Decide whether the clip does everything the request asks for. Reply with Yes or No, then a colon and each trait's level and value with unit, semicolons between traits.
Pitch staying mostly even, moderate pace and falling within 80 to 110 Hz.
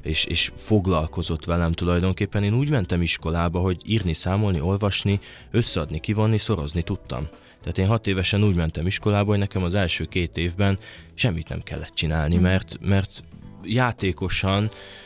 No: average, 3.3 semitones; average, 145 wpm; very low, 95 Hz